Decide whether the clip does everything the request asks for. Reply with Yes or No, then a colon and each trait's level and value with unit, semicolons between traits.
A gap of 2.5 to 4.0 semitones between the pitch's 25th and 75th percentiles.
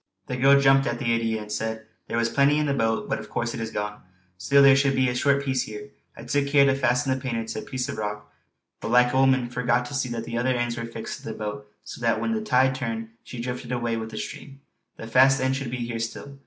Yes: average, 2.9 semitones